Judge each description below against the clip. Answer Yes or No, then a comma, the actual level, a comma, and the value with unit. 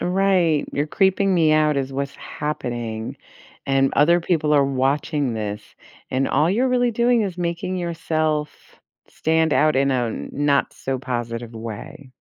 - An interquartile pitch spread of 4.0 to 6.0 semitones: Yes, average, 4.5 semitones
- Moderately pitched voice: Yes, medium, 150 Hz